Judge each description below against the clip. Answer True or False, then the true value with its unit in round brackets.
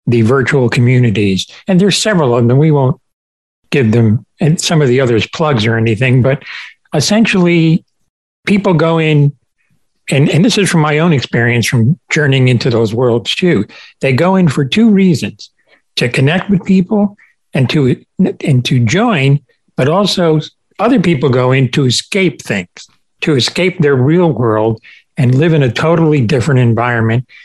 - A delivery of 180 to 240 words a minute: False (165 wpm)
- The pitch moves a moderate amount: False (5.8 semitones)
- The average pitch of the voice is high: False (145 Hz)